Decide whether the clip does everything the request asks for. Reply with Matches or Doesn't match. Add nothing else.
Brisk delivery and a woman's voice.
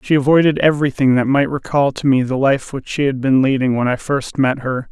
Doesn't match